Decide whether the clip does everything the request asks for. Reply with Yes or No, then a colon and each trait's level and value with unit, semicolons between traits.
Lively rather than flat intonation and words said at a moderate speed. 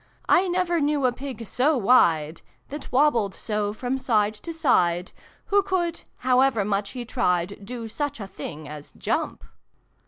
Yes: wide, 6.4 semitones; average, 155 wpm